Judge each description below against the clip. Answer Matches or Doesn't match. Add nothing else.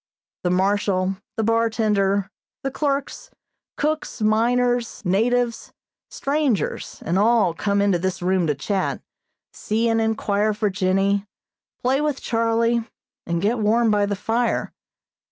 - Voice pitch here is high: Matches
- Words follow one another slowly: Matches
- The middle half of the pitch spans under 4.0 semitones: Matches